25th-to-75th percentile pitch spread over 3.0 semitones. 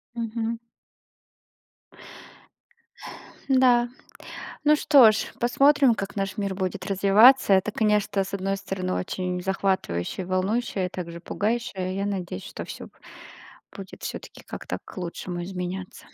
Yes: average, 3.6 semitones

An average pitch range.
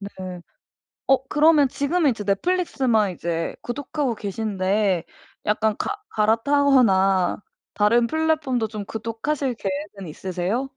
No: wide, 5.9 semitones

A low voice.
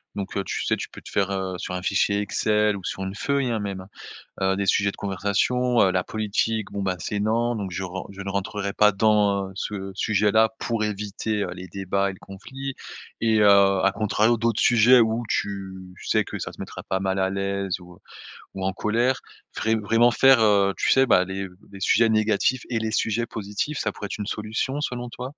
Yes: low, 105 Hz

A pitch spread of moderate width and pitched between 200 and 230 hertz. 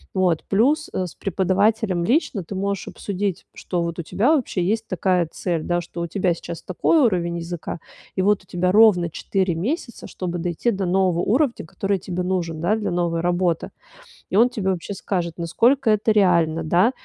No: average, 3.2 semitones; medium, 185 Hz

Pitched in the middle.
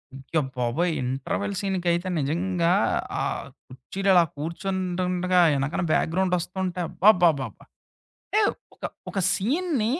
Yes: medium, 180 Hz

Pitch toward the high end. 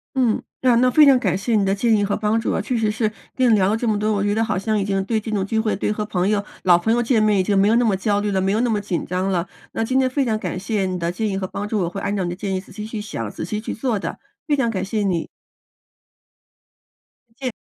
Yes: high, 210 Hz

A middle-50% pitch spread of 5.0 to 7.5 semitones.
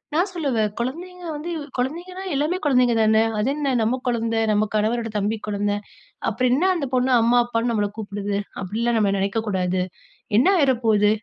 No: average, 4.6 semitones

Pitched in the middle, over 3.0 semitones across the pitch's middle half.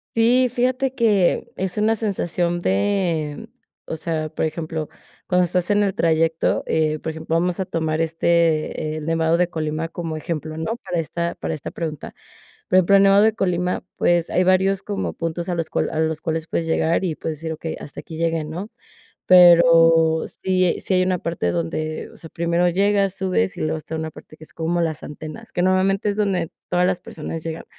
No: medium, 170 Hz; average, 2.7 semitones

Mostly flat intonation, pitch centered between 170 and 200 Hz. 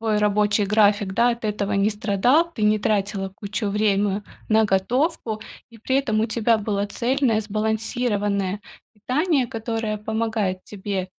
No: narrow, 2.0 semitones; high, 215 Hz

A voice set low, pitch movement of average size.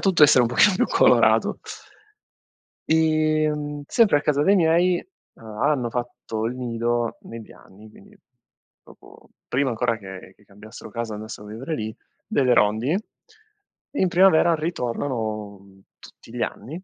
No: low, 125 Hz; wide, 6.0 semitones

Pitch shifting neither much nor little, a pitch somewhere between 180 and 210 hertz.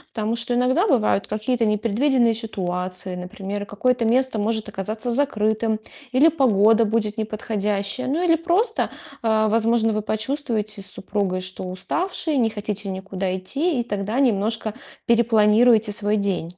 No: average, 3.2 semitones; high, 220 Hz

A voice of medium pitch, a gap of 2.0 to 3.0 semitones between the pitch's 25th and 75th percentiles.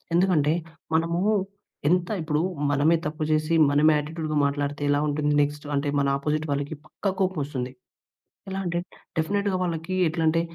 Yes: medium, 155 Hz; narrow, 2.6 semitones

